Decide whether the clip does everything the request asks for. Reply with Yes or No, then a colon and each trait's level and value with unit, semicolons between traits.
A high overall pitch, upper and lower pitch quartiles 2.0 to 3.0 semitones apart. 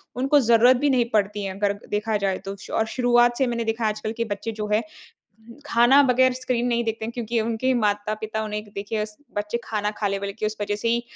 Yes: high, 225 Hz; narrow, 2.4 semitones